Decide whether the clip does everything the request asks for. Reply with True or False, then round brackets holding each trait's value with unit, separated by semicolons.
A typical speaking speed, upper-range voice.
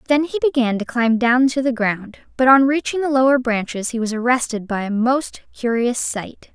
False (210 wpm; 245 Hz)